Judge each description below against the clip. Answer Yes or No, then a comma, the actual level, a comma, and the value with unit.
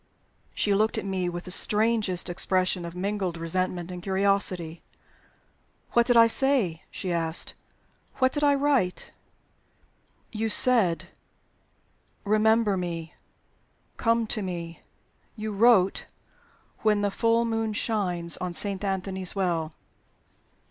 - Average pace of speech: No, slow, 120 wpm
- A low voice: No, high, 195 Hz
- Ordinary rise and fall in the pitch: Yes, average, 3.9 semitones